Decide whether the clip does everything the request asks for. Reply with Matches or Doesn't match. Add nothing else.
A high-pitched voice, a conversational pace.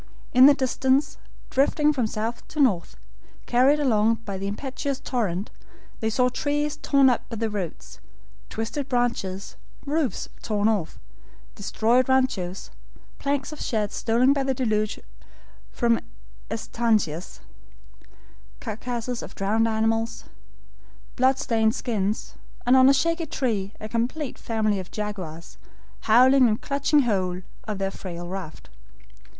Doesn't match